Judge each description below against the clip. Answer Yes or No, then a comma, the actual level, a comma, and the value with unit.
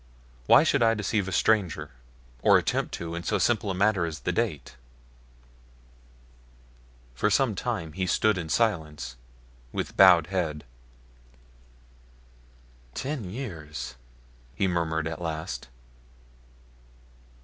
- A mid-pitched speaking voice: No, very low, 90 Hz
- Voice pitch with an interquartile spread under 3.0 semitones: No, average, 5.0 semitones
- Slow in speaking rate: Yes, slow, 115 wpm